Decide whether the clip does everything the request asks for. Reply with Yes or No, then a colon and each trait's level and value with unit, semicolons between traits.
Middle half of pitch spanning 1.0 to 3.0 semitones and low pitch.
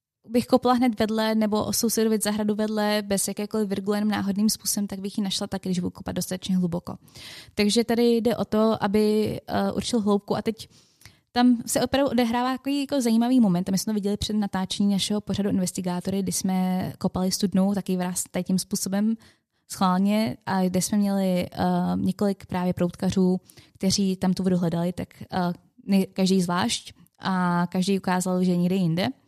No: narrow, 2.6 semitones; high, 200 Hz